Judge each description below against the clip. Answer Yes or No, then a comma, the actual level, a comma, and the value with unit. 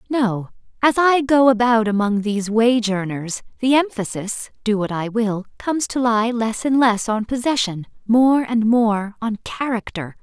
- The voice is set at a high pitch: Yes, high, 230 Hz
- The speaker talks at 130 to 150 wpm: Yes, average, 140 wpm